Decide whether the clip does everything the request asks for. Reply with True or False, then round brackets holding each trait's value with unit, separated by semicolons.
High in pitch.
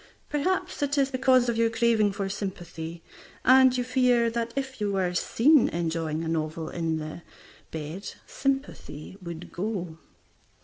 True (210 Hz)